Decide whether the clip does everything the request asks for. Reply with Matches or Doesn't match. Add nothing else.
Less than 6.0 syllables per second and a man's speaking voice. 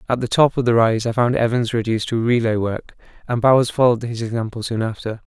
Doesn't match